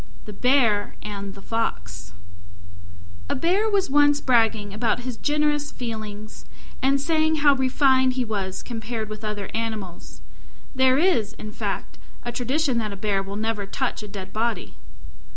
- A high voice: Yes, high, 230 Hz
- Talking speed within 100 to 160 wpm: Yes, average, 150 wpm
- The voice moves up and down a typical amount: Yes, average, 4.4 semitones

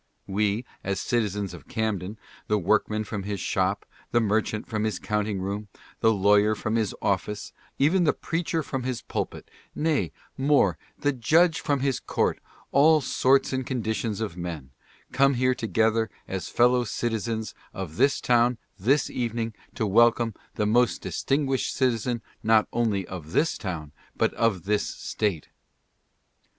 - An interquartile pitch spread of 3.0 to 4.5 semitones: Yes, average, 3.8 semitones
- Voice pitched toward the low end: Yes, low, 110 Hz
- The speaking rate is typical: Yes, average, 160 wpm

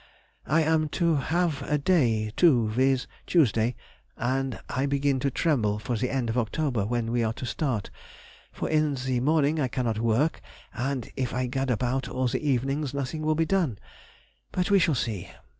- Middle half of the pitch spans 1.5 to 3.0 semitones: No, average, 4.1 semitones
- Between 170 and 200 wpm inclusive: Yes, average, 180 wpm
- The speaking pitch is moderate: No, low, 130 Hz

